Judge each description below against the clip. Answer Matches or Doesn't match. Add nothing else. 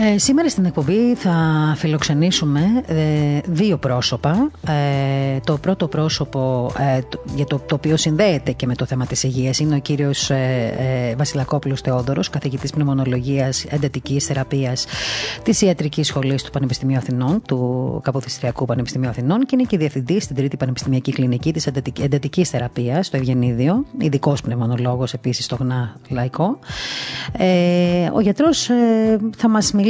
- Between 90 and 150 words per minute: Matches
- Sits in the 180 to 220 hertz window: Doesn't match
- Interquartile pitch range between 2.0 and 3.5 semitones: Doesn't match